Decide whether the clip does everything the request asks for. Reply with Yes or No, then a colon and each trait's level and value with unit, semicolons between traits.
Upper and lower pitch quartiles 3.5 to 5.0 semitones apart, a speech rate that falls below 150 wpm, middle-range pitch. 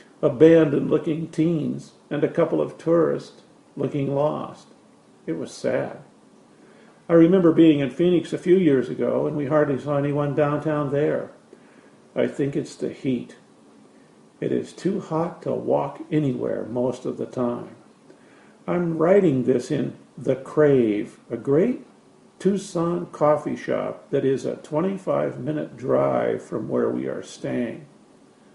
No: average, 2.8 semitones; average, 140 wpm; medium, 150 Hz